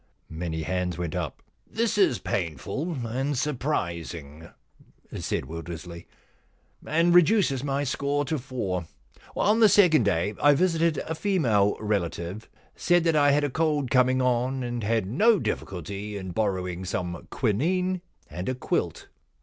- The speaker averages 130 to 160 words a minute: Yes, average, 150 wpm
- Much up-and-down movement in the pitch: Yes, wide, 9.0 semitones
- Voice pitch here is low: Yes, low, 125 Hz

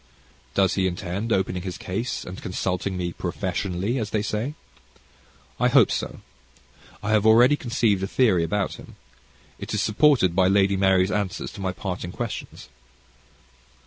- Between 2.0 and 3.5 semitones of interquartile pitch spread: Yes, average, 3.1 semitones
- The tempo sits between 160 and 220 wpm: No, average, 150 wpm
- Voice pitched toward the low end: Yes, low, 100 Hz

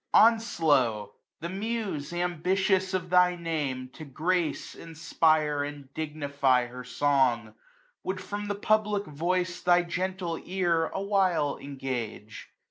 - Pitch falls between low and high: Yes, medium, 165 Hz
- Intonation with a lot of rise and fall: No, average, 4.7 semitones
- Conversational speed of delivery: No, slow, 125 wpm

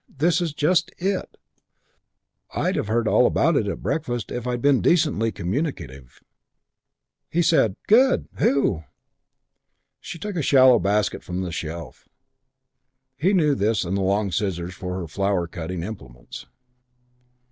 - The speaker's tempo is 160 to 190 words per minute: No, average, 140 wpm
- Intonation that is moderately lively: No, wide, 8.7 semitones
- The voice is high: No, low, 110 Hz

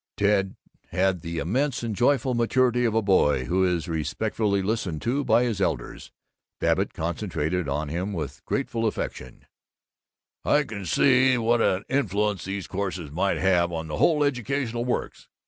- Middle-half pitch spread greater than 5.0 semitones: Yes, wide, 5.5 semitones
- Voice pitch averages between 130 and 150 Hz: No, low, 100 Hz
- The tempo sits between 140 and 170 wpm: Yes, average, 155 wpm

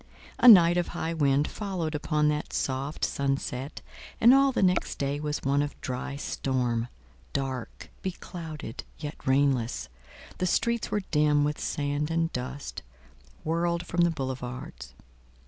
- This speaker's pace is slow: Yes, slow, 130 wpm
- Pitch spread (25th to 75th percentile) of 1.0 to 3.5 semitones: No, average, 4.0 semitones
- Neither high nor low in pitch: Yes, medium, 145 Hz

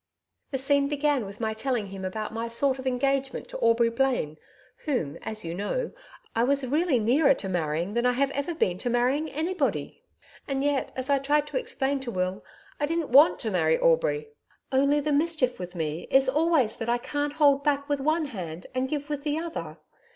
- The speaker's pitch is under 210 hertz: No, very high, 270 Hz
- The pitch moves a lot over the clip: No, average, 4.2 semitones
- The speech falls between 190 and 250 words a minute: Yes, average, 200 wpm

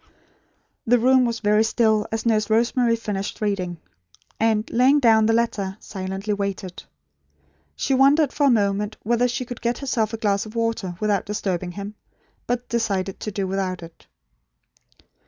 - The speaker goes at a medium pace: Yes, average, 160 wpm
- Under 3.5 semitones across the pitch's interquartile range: Yes, average, 3.0 semitones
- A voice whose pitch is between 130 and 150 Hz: No, high, 215 Hz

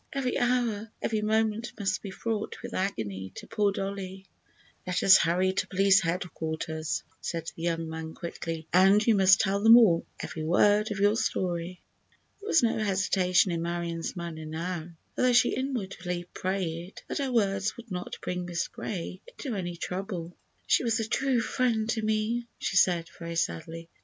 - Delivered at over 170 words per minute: No, average, 165 wpm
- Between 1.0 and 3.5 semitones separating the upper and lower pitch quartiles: No, average, 4.2 semitones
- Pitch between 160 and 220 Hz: Yes, high, 190 Hz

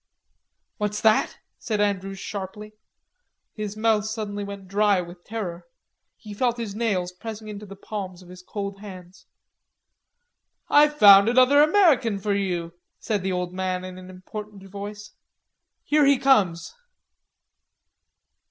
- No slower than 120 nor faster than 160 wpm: Yes, slow, 135 wpm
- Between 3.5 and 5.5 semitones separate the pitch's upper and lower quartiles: No, average, 2.7 semitones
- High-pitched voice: Yes, high, 205 Hz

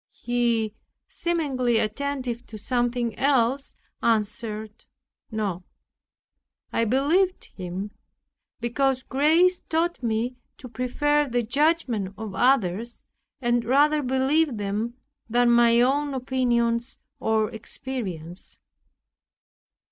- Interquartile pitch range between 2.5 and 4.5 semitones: Yes, average, 3.6 semitones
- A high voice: Yes, high, 240 Hz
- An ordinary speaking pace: No, slow, 95 wpm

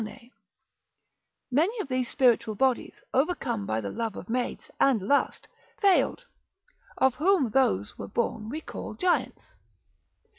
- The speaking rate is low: Yes, slow, 125 wpm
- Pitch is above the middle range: Yes, very high, 255 Hz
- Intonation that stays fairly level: No, wide, 5.4 semitones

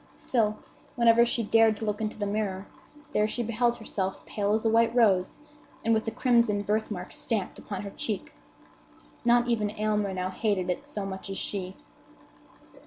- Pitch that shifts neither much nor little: No, narrow, 2.3 semitones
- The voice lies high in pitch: Yes, high, 215 Hz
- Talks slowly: No, average, 175 wpm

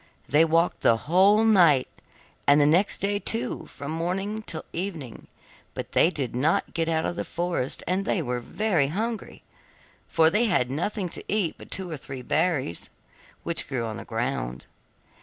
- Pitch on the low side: No, medium, 165 Hz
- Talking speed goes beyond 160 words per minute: Yes, average, 175 wpm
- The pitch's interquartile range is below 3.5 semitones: No, wide, 5.4 semitones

